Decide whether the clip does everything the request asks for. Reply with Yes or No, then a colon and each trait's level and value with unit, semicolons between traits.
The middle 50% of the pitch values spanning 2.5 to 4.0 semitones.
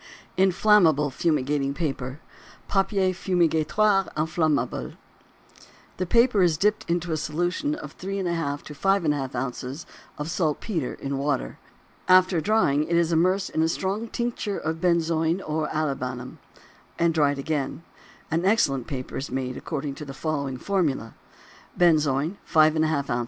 No: average, 4.5 semitones